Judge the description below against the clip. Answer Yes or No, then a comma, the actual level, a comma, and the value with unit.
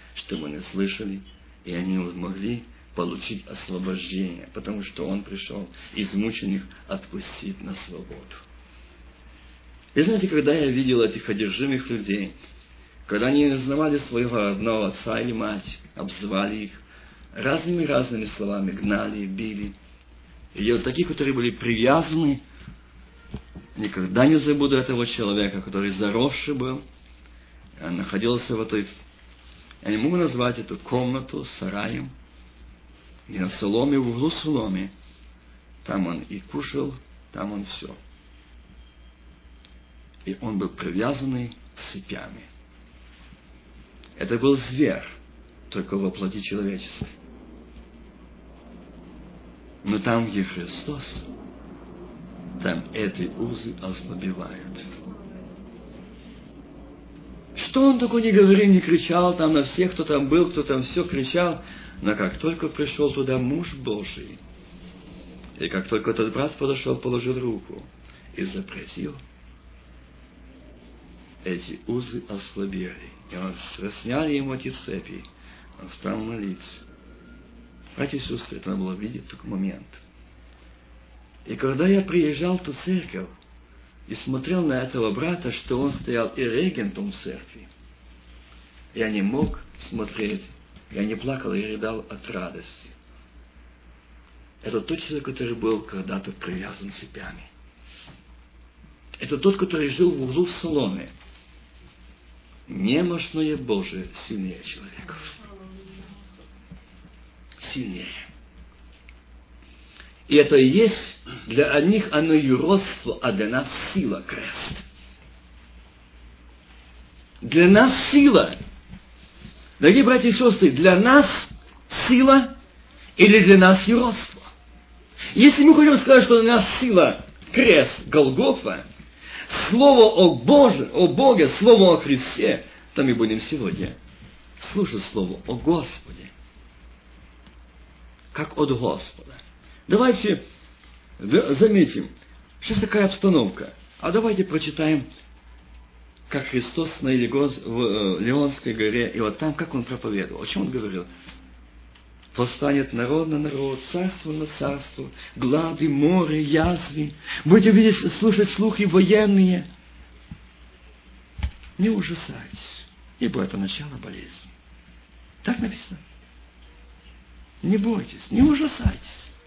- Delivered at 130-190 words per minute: No, slow, 110 wpm